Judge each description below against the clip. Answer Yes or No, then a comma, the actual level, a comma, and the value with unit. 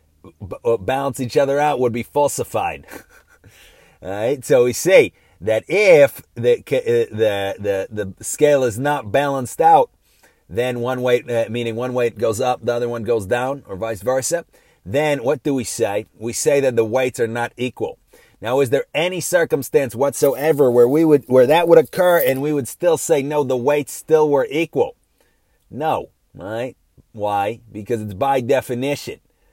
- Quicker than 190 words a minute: No, average, 175 wpm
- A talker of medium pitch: No, low, 130 Hz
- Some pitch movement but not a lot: Yes, average, 3.9 semitones